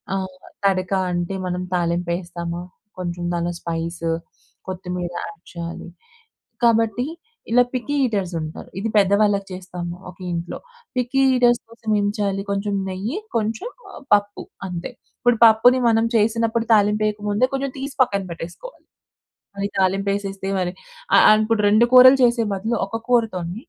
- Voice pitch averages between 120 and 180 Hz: No, high, 200 Hz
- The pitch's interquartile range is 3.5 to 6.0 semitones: Yes, average, 4.1 semitones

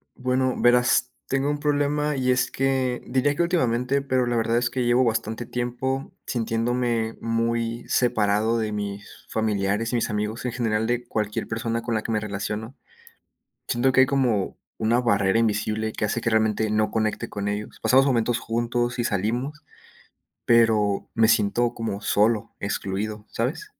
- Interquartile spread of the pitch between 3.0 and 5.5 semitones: No, narrow, 2.6 semitones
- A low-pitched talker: Yes, low, 115 Hz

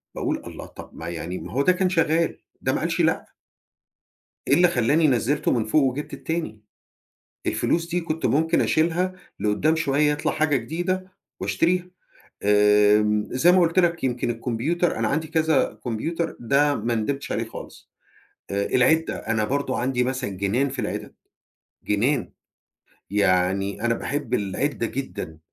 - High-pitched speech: No, low, 135 Hz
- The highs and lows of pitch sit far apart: Yes, wide, 7.0 semitones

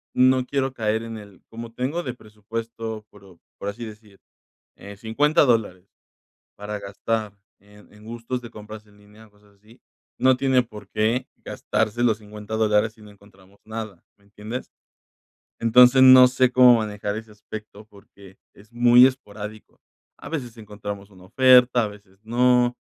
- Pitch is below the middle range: Yes, low, 110 Hz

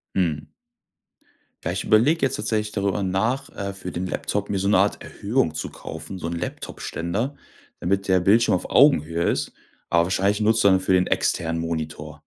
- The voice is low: Yes, very low, 95 Hz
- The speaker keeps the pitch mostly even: No, average, 3.7 semitones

